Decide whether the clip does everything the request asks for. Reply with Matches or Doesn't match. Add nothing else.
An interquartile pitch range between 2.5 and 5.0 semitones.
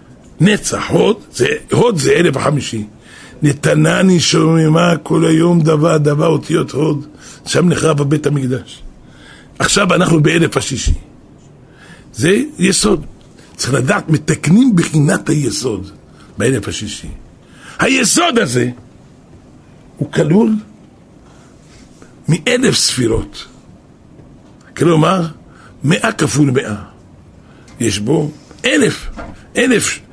Doesn't match